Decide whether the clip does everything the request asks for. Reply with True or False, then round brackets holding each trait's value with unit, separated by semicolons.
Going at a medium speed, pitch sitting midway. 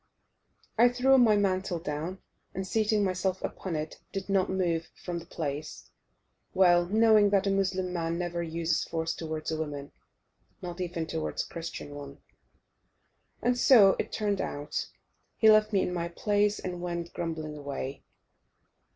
True (150 wpm; 180 Hz)